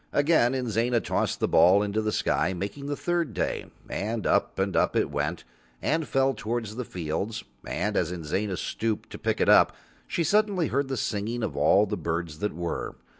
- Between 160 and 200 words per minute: Yes, average, 190 wpm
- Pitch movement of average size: No, wide, 6.0 semitones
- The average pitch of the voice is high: No, low, 110 Hz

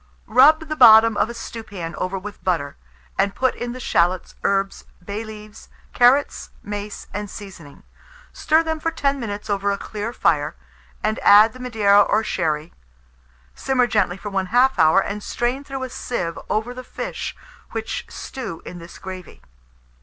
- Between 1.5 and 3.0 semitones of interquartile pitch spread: No, average, 4.2 semitones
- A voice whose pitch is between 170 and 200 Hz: No, high, 210 Hz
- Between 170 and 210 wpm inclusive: No, average, 160 wpm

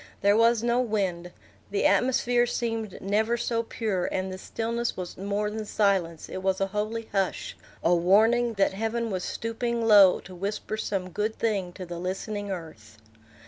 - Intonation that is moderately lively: Yes, average, 3.4 semitones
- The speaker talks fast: No, average, 170 wpm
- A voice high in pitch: Yes, high, 205 Hz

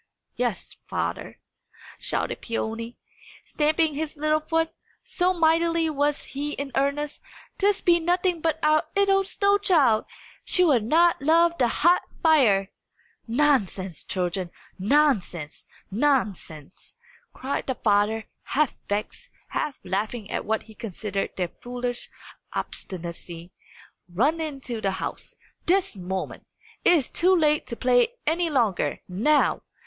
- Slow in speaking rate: Yes, slow, 125 wpm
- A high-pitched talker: Yes, very high, 280 Hz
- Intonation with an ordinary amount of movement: No, wide, 7.3 semitones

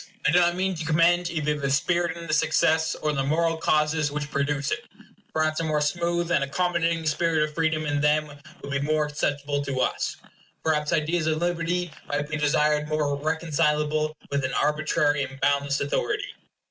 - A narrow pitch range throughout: Yes, narrow, 2.2 semitones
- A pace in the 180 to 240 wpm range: Yes, average, 185 wpm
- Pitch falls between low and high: Yes, medium, 155 Hz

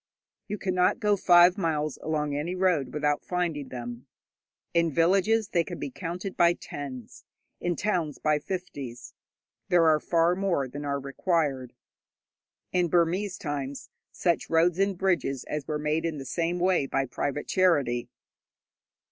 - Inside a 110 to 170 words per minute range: Yes, average, 155 wpm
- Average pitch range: Yes, average, 3.9 semitones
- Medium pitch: Yes, medium, 165 Hz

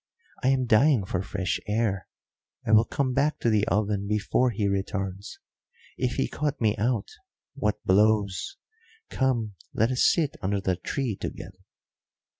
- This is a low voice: Yes, low, 110 Hz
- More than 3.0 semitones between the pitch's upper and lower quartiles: Yes, average, 4.3 semitones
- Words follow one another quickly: No, average, 150 wpm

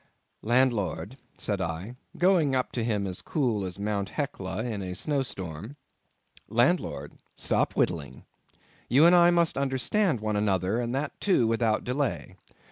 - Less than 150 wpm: Yes, average, 140 wpm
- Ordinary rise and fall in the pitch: No, wide, 5.8 semitones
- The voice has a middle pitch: No, low, 120 Hz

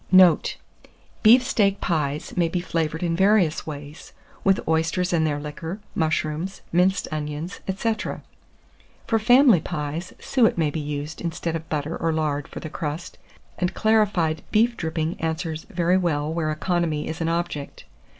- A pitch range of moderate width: Yes, average, 3.0 semitones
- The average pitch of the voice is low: No, medium, 165 Hz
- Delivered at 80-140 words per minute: No, average, 150 wpm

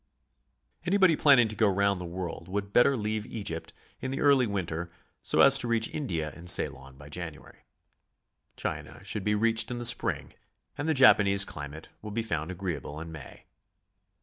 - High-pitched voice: No, low, 100 Hz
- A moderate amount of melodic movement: No, wide, 5.9 semitones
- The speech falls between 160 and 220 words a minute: Yes, average, 175 wpm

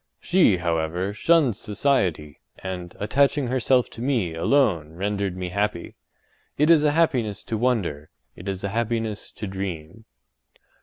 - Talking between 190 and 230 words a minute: No, average, 140 wpm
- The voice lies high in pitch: No, low, 105 Hz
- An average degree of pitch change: No, wide, 6.0 semitones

